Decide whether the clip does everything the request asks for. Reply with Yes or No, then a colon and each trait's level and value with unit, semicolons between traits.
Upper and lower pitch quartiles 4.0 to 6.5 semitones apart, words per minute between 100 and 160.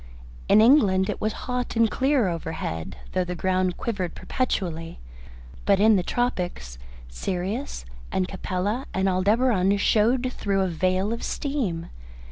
Yes: average, 4.3 semitones; slow, 135 wpm